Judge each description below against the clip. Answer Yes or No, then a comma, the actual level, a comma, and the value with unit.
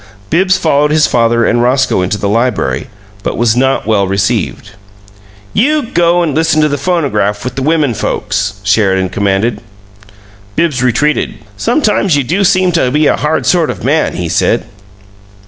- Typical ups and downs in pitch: No, wide, 7.1 semitones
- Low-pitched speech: Yes, low, 130 Hz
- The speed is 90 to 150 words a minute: No, average, 165 wpm